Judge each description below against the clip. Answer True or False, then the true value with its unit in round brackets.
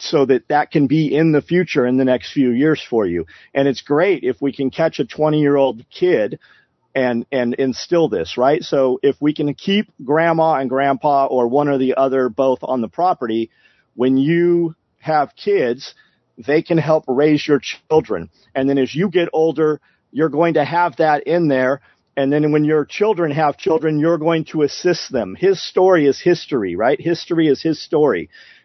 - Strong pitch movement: False (3.3 semitones)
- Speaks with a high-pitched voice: False (150 Hz)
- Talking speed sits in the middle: True (190 wpm)